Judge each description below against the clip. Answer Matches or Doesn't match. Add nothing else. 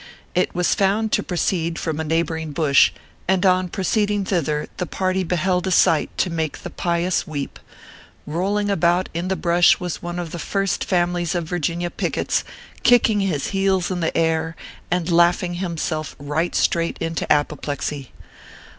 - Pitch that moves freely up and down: Doesn't match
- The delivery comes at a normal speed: Matches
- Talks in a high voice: Doesn't match